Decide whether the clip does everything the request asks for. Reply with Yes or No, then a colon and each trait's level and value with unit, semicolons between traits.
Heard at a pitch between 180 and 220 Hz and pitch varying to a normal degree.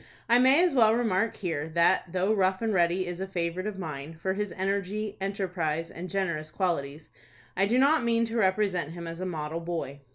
Yes: medium, 185 Hz; average, 3.9 semitones